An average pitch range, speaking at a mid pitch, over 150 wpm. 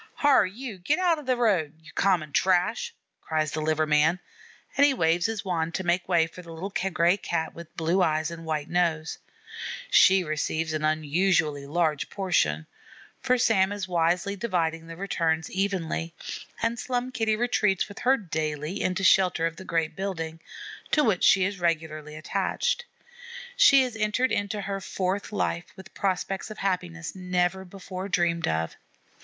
Yes: average, 3.6 semitones; medium, 180 Hz; average, 165 wpm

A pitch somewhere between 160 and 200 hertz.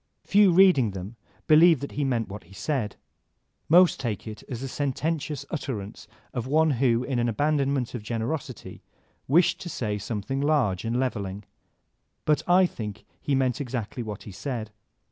No: low, 130 Hz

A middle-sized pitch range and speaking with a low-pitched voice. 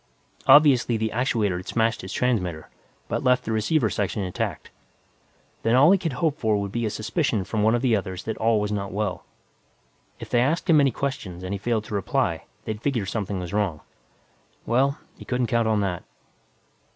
Yes: average, 4.0 semitones; low, 110 Hz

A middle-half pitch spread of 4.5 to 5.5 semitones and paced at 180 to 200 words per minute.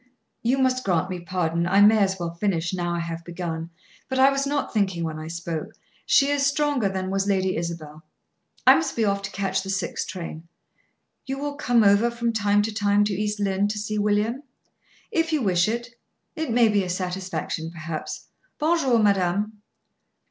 Yes: average, 5.0 semitones; average, 190 wpm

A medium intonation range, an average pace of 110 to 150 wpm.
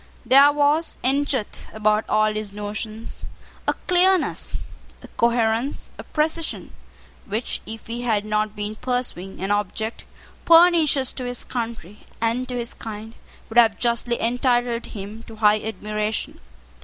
Yes: average, 3.1 semitones; average, 140 wpm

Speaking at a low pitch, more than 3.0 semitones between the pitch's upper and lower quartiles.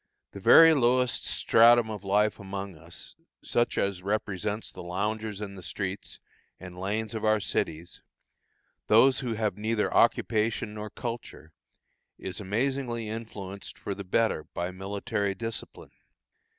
No: low, 105 Hz; average, 2.7 semitones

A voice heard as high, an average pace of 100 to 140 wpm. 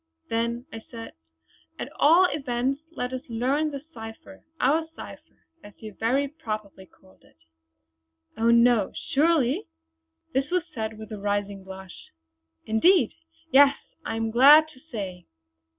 Yes: high, 235 Hz; slow, 135 wpm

